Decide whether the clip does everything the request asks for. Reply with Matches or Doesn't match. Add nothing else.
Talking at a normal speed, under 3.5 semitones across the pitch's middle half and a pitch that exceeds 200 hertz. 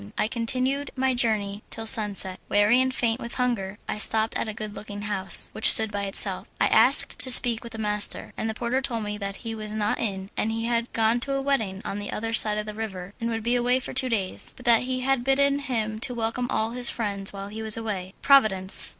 Doesn't match